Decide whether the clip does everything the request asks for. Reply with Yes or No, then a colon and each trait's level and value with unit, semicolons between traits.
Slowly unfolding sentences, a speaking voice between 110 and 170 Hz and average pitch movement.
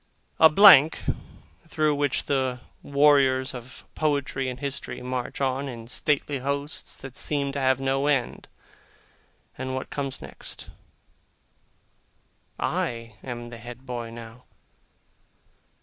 No: slow, 120 wpm; low, 135 Hz; narrow, 2.2 semitones